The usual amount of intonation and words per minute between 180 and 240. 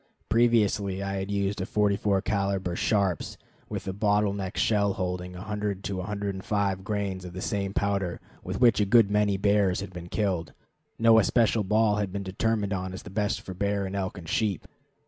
No: narrow, 1.6 semitones; average, 185 wpm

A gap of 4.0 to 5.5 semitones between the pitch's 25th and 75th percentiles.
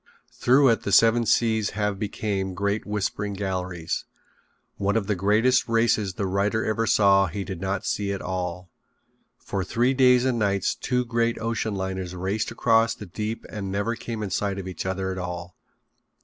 No: average, 3.0 semitones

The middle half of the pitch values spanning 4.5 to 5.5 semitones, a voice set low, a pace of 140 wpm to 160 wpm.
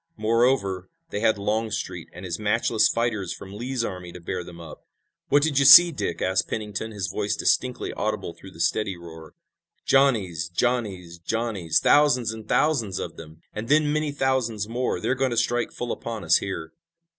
No: average, 4.9 semitones; low, 105 Hz; average, 180 wpm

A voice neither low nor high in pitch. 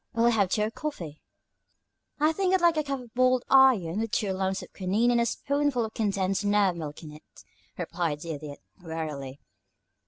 No: high, 210 Hz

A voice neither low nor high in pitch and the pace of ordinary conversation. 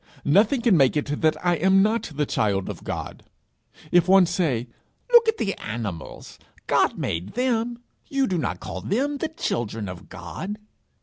Yes: medium, 180 Hz; average, 170 wpm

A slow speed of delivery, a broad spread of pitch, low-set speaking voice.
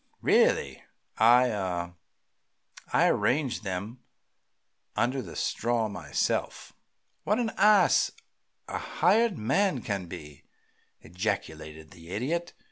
Yes: slow, 100 wpm; wide, 7.5 semitones; low, 110 Hz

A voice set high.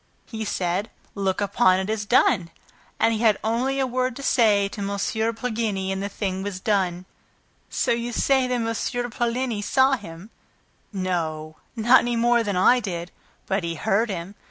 Yes: high, 210 Hz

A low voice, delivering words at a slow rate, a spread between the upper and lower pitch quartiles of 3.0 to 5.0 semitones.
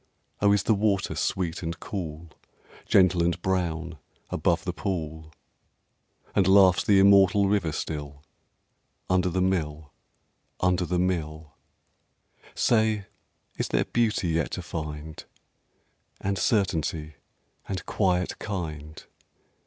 Yes: very low, 90 Hz; slow, 115 wpm; average, 3.5 semitones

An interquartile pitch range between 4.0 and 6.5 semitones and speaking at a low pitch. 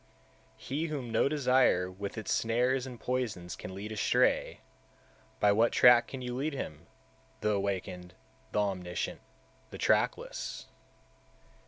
Yes: average, 4.6 semitones; low, 110 Hz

